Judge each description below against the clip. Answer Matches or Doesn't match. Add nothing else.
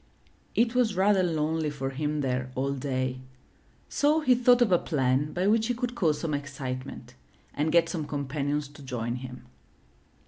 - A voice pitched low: Doesn't match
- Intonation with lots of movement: Matches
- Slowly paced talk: Doesn't match